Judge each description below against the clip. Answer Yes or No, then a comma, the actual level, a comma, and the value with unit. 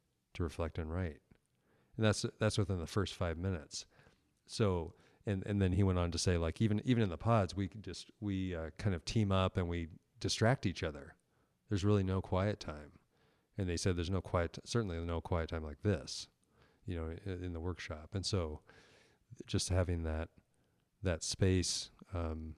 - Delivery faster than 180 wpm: Yes, average, 195 wpm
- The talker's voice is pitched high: No, very low, 95 Hz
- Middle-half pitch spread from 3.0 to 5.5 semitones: Yes, average, 3.6 semitones